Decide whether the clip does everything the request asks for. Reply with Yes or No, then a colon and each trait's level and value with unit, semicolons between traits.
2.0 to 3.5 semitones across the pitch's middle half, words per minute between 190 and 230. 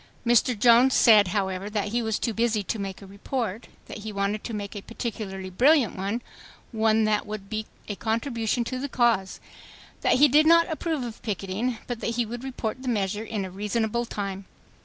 Yes: average, 3.0 semitones; average, 200 wpm